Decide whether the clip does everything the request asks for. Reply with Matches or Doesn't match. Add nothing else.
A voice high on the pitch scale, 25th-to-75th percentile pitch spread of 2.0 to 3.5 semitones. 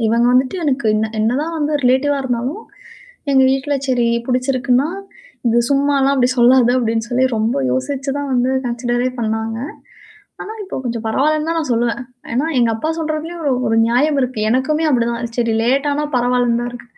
Matches